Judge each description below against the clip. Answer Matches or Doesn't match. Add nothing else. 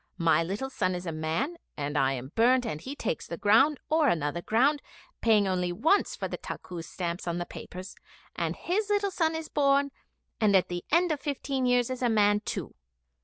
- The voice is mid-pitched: Doesn't match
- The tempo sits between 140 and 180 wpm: Doesn't match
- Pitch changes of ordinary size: Doesn't match